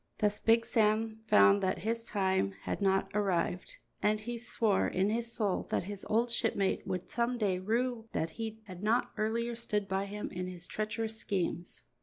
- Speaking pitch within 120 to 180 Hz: No, high, 210 Hz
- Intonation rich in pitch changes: No, average, 3.1 semitones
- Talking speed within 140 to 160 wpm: No, average, 180 wpm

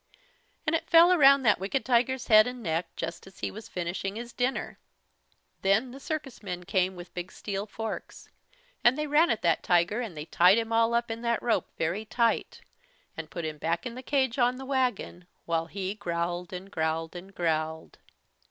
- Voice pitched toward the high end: Yes, high, 210 Hz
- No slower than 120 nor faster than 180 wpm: No, average, 195 wpm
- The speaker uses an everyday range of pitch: No, wide, 6.0 semitones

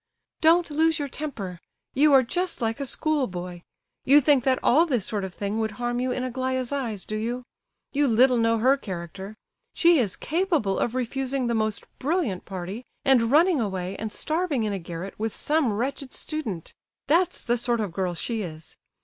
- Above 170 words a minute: Yes, average, 185 wpm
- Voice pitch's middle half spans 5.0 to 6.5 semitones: Yes, wide, 5.6 semitones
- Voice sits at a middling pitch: No, high, 245 Hz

